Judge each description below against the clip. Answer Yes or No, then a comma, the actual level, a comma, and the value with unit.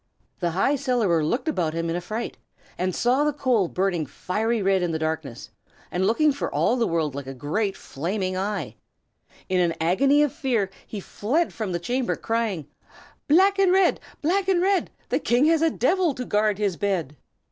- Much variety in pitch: Yes, wide, 7.9 semitones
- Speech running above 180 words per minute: Yes, average, 190 wpm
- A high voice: Yes, high, 210 Hz